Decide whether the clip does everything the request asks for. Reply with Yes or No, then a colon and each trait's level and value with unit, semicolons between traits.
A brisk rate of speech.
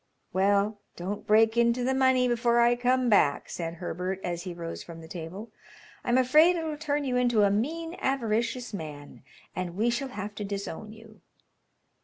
No: average, 175 wpm